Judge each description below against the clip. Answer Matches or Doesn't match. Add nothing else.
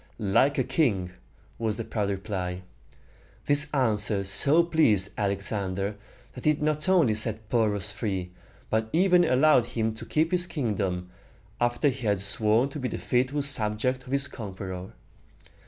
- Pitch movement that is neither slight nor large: Doesn't match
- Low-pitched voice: Matches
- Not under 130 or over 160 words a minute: Matches